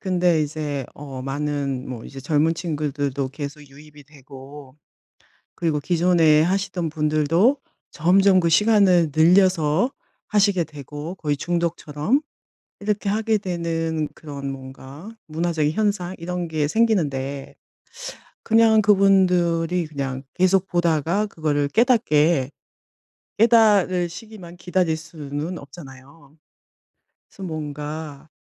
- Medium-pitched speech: Yes, medium, 160 Hz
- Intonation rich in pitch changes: No, average, 4.0 semitones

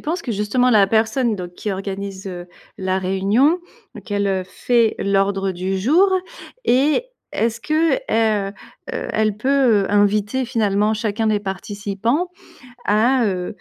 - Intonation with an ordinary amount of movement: Yes, average, 3.7 semitones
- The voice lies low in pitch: No, high, 210 Hz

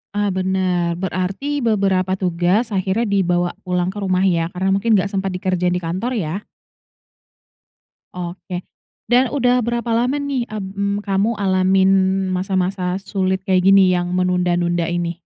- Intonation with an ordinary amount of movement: No, narrow, 2.0 semitones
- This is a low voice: No, high, 190 Hz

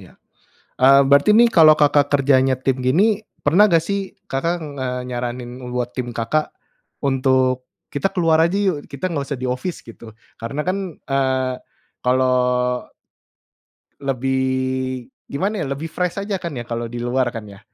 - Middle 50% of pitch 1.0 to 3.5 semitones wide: No, average, 4.3 semitones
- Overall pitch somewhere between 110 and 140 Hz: Yes, low, 135 Hz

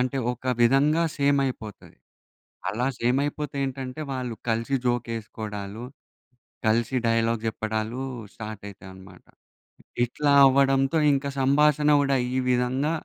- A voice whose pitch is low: Yes, low, 125 Hz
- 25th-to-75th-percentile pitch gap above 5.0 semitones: No, average, 3.6 semitones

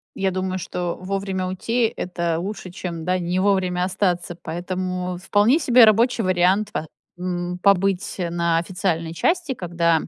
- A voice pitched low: No, medium, 185 Hz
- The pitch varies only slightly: Yes, narrow, 2.0 semitones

